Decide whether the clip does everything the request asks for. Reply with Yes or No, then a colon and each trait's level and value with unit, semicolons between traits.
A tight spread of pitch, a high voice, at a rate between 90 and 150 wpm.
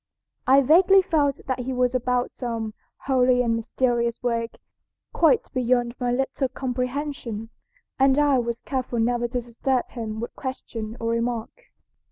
Yes: narrow, 2.1 semitones; very high, 250 Hz; average, 145 wpm